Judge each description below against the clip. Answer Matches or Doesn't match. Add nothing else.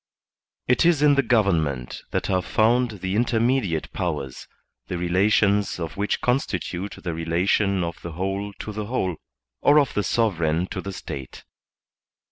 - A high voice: Doesn't match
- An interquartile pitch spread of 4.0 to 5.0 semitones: Matches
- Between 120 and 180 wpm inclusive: Matches